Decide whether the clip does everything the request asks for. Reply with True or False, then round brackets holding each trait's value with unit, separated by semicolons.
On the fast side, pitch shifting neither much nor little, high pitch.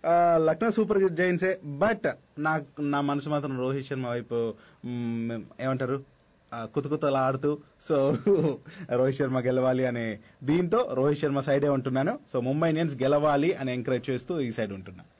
False (130 wpm; 3.1 semitones; 140 Hz)